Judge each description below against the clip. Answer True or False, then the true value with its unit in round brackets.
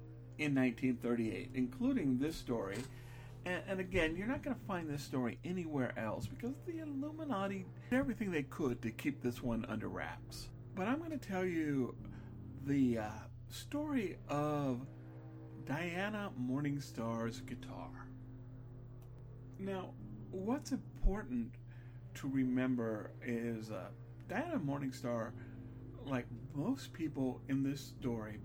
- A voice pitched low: True (125 Hz)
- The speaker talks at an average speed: False (120 wpm)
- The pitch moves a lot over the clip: False (3.3 semitones)